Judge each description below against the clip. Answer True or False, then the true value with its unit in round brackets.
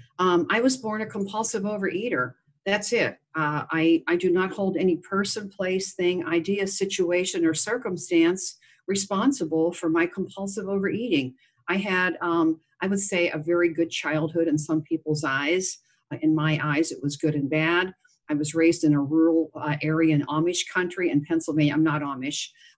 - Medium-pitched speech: True (170 Hz)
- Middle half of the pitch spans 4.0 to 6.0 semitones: False (3.1 semitones)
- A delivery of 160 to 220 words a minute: True (175 wpm)